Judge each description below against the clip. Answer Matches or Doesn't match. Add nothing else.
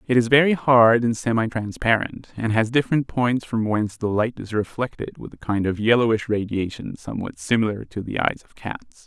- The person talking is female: Doesn't match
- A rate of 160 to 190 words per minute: Doesn't match